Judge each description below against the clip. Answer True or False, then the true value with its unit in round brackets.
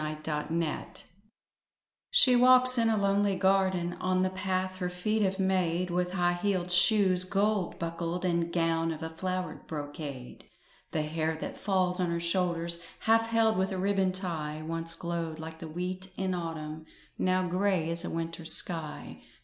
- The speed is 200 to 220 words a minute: False (165 wpm)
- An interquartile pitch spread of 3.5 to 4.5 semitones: False (2.4 semitones)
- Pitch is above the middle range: False (180 Hz)